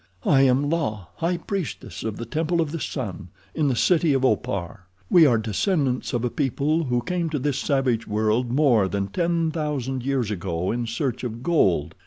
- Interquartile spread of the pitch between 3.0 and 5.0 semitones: No, wide, 5.6 semitones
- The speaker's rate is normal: Yes, average, 190 wpm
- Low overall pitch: Yes, low, 130 Hz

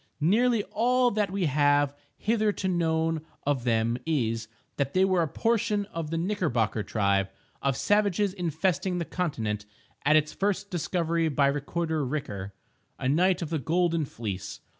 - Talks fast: No, average, 150 wpm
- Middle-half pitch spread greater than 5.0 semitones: Yes, wide, 5.4 semitones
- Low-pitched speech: No, medium, 160 Hz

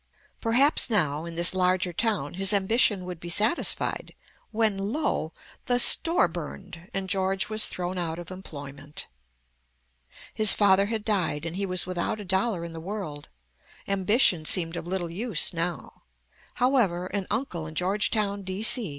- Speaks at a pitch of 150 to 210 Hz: Yes, high, 190 Hz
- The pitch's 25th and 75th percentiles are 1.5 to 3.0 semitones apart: No, average, 3.6 semitones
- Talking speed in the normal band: Yes, average, 150 wpm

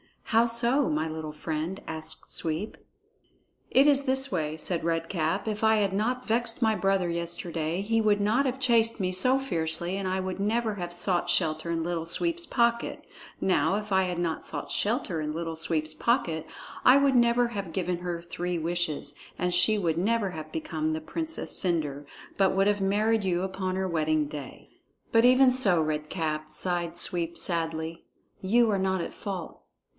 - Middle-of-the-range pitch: Yes, medium, 180 Hz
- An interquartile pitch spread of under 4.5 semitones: No, average, 5.2 semitones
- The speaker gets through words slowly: No, average, 180 wpm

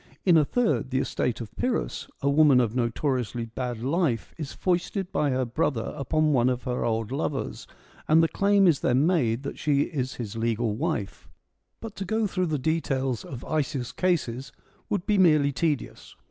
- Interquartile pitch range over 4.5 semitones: Yes, average, 5.1 semitones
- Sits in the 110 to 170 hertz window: Yes, medium, 140 Hz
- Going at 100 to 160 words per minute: No, average, 185 wpm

